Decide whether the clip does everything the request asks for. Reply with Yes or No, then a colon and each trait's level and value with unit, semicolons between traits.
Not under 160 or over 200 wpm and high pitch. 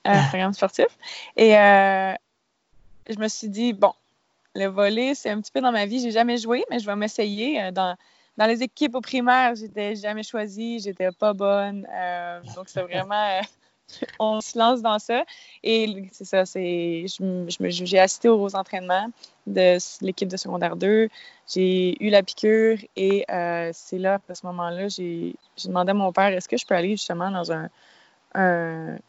Yes: average, 185 wpm; high, 200 Hz